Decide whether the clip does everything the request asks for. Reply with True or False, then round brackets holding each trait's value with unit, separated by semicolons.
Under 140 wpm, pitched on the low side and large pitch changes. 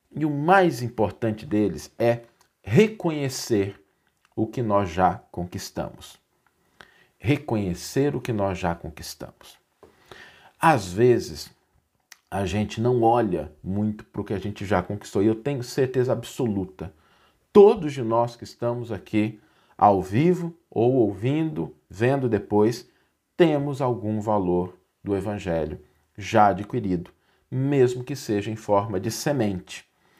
False (125 wpm; 110 Hz; 4.3 semitones)